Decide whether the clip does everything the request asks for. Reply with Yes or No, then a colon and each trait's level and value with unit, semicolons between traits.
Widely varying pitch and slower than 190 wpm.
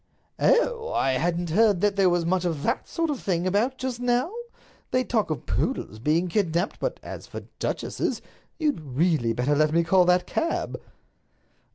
Yes: wide, 7.0 semitones; average, 170 wpm